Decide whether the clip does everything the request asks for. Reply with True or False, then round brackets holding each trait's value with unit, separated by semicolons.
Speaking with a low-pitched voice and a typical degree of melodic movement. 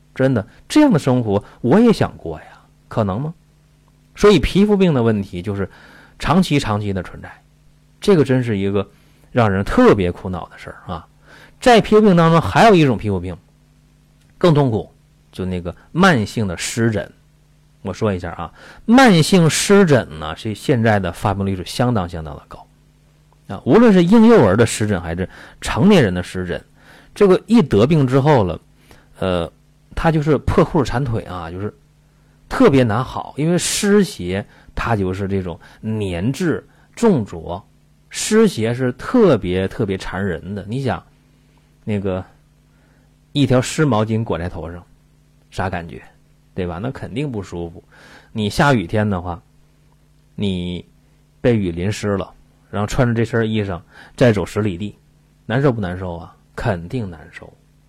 False (120 Hz; 7.5 semitones)